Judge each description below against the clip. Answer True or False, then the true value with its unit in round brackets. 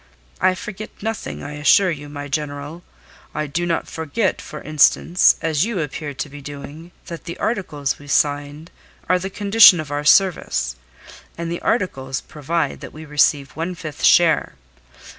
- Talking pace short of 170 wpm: True (160 wpm)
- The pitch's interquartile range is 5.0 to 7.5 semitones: False (3.6 semitones)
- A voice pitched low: False (155 Hz)